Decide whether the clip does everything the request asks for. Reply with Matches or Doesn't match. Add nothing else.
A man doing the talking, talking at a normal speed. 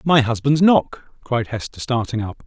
Matches